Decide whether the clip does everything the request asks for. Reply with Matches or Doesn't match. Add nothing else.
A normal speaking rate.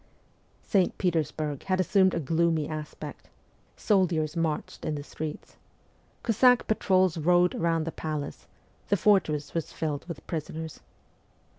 Doesn't match